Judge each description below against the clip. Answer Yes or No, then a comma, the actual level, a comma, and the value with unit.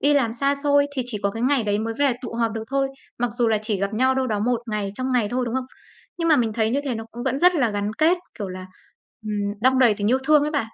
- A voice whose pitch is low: No, high, 240 Hz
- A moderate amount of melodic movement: Yes, average, 4.0 semitones